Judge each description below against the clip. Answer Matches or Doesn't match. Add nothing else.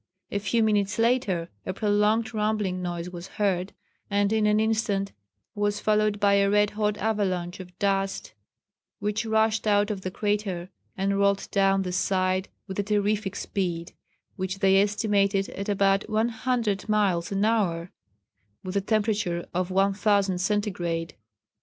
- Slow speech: Doesn't match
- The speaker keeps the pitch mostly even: Matches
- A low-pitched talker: Doesn't match